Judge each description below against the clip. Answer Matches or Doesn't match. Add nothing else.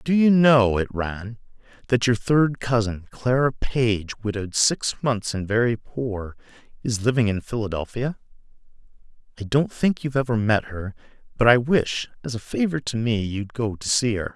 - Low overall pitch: Matches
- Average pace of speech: Matches